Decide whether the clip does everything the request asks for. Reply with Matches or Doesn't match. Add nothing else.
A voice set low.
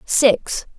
Doesn't match